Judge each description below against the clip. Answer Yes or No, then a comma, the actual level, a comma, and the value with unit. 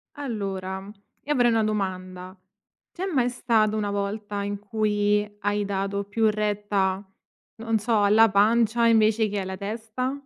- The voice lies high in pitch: Yes, high, 210 Hz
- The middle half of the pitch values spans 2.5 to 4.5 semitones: No, narrow, 2.0 semitones